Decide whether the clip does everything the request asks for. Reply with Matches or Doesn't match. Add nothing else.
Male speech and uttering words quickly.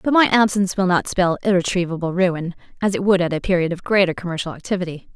Doesn't match